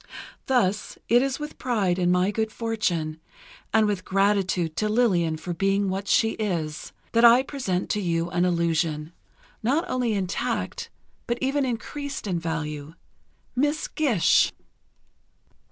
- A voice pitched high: Yes, high, 200 Hz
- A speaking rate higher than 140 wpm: No, slow, 135 wpm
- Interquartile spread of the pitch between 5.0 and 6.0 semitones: Yes, wide, 5.6 semitones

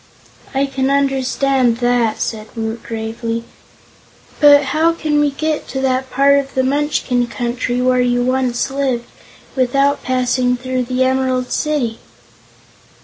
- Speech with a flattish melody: Yes, narrow, 2.1 semitones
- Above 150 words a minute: No, slow, 135 wpm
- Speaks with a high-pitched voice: Yes, very high, 255 Hz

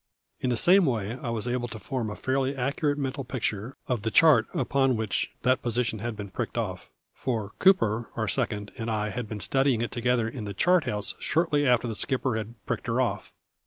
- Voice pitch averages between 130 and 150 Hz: No, low, 120 Hz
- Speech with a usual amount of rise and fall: Yes, average, 3.5 semitones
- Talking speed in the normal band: No, fast, 210 wpm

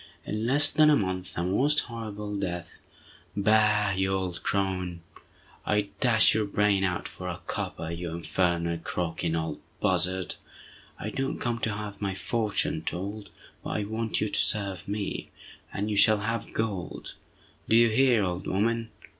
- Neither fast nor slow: Yes, average, 155 wpm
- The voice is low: Yes, low, 100 Hz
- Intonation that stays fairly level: No, average, 3.2 semitones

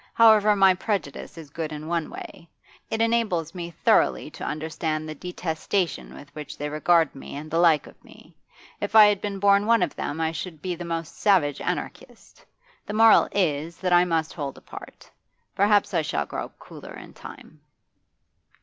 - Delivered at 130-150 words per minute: No, average, 180 wpm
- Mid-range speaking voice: Yes, medium, 170 Hz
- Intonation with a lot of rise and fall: No, average, 4.3 semitones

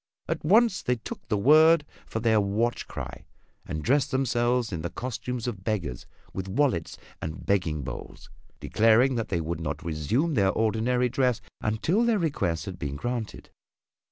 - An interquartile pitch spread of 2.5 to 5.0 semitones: No, wide, 5.4 semitones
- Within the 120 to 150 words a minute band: No, average, 160 wpm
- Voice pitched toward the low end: Yes, low, 115 Hz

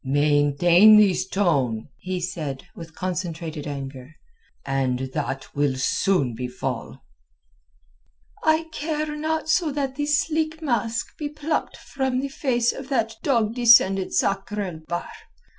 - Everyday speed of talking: No, slow, 125 wpm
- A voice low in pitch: No, high, 195 Hz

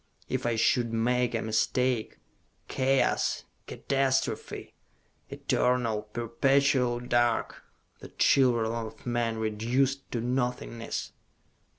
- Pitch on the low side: Yes, low, 120 Hz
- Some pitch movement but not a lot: No, narrow, 2.0 semitones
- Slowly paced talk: Yes, slow, 90 wpm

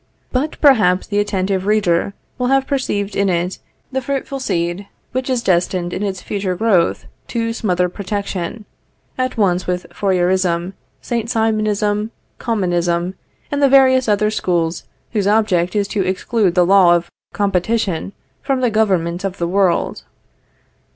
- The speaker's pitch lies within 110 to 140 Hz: No, high, 200 Hz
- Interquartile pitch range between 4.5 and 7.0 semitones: No, average, 3.9 semitones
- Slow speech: No, average, 145 wpm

